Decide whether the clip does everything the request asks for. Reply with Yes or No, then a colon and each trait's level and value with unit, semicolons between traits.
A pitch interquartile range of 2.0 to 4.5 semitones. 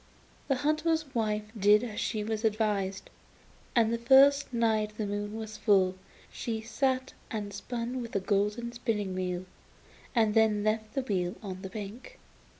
Yes: narrow, 2.5 semitones